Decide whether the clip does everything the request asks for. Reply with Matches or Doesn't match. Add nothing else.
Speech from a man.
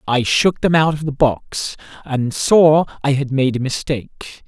Matches